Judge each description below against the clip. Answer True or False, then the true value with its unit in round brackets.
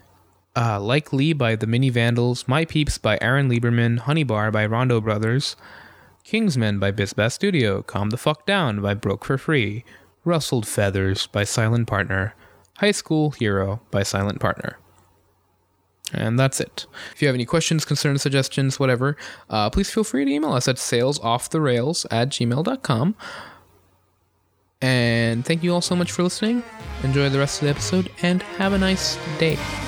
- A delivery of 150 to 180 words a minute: True (165 wpm)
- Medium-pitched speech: False (120 Hz)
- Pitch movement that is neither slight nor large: False (6.8 semitones)